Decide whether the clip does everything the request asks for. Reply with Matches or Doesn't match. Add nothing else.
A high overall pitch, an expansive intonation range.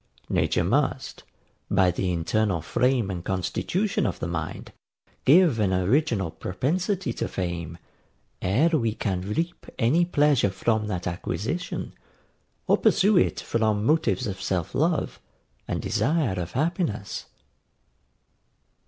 Doesn't match